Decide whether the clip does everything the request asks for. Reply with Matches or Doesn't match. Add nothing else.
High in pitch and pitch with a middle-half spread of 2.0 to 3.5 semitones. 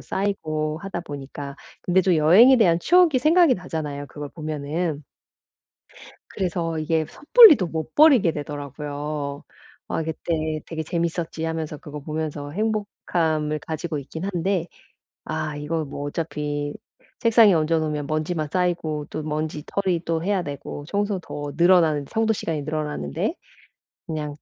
Doesn't match